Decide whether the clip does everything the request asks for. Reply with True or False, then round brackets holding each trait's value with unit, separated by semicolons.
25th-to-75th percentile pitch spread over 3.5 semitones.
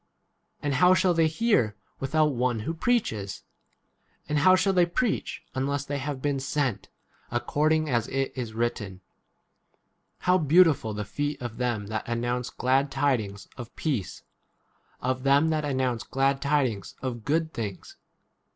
True (4.4 semitones)